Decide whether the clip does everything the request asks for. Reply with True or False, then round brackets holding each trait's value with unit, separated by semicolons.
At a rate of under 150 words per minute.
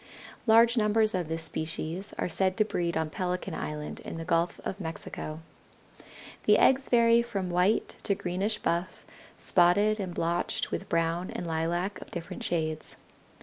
False (155 wpm)